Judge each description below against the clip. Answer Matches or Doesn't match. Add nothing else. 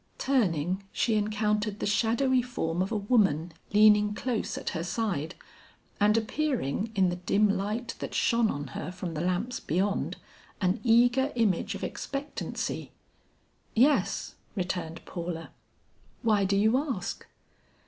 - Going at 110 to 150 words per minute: Matches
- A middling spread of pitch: Matches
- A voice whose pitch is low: Doesn't match